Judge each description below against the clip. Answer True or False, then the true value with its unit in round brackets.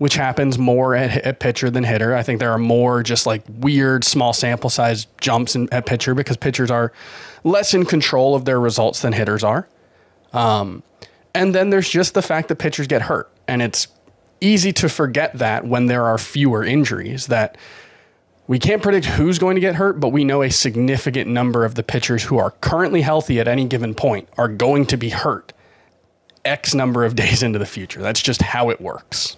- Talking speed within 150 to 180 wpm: False (205 wpm)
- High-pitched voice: False (125 Hz)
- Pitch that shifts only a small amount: False (3.5 semitones)